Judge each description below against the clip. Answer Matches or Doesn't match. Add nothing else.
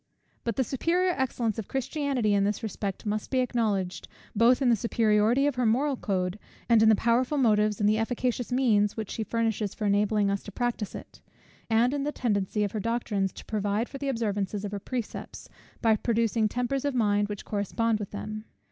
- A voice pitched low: Doesn't match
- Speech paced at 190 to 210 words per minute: Matches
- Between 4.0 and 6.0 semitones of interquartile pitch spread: Doesn't match